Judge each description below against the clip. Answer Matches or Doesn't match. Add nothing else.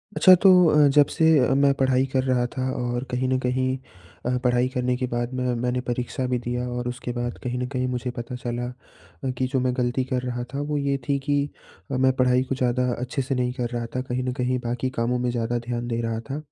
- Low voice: Matches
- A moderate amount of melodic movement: Doesn't match